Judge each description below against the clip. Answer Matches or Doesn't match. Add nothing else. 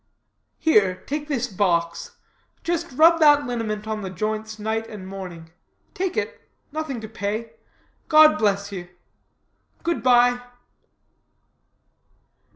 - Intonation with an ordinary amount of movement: Doesn't match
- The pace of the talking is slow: Matches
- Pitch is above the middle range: Matches